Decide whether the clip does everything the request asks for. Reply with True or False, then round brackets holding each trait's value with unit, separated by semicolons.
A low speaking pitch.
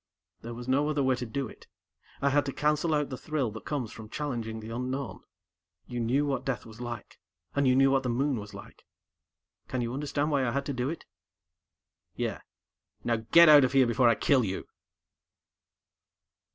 True (130 Hz)